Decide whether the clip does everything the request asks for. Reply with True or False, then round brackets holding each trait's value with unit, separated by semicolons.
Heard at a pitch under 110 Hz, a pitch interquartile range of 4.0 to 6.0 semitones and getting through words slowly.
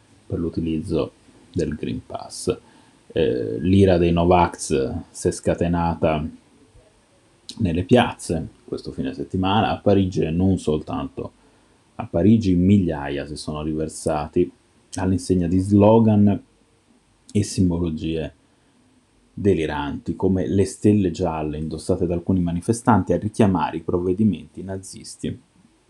False (90 Hz; 2.9 semitones; 110 wpm)